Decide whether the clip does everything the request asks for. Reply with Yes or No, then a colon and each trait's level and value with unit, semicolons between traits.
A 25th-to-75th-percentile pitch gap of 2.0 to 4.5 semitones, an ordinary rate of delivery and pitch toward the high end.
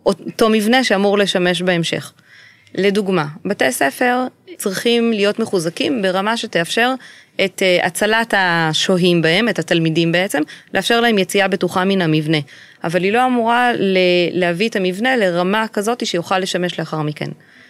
Yes: average, 4.2 semitones; average, 130 wpm; high, 195 Hz